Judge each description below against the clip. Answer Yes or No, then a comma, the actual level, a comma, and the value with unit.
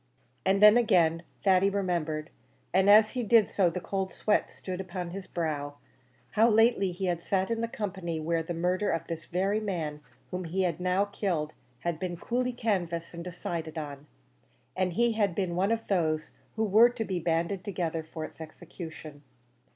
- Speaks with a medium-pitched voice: Yes, medium, 180 Hz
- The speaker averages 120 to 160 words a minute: No, average, 180 wpm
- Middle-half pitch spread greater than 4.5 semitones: No, average, 3.4 semitones